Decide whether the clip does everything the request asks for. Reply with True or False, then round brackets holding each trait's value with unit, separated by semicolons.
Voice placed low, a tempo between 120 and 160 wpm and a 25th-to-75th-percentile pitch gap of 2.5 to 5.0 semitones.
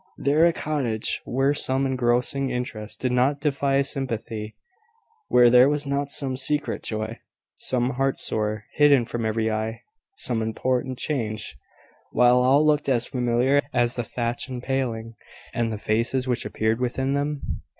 True (125 Hz; 150 wpm; 2.9 semitones)